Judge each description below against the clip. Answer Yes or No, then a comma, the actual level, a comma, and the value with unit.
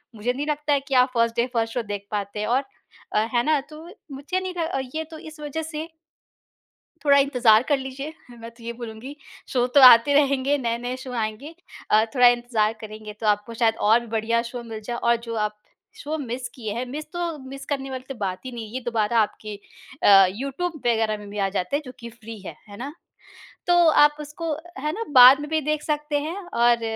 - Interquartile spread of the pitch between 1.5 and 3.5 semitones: No, average, 4.4 semitones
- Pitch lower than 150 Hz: No, high, 245 Hz